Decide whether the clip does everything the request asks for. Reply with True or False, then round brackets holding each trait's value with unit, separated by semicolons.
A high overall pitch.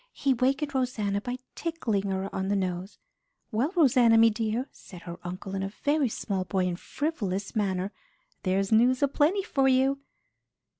True (220 Hz)